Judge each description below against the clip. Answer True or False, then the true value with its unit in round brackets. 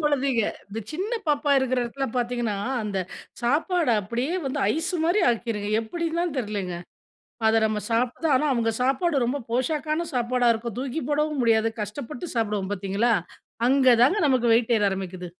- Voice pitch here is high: True (245 Hz)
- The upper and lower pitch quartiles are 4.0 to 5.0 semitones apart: True (4.7 semitones)